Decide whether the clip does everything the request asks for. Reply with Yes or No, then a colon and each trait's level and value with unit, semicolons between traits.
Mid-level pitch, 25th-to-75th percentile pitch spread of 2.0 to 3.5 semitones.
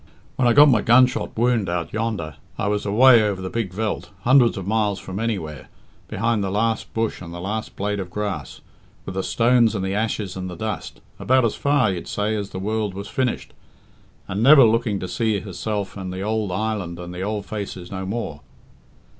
No: low, 105 Hz; average, 3.2 semitones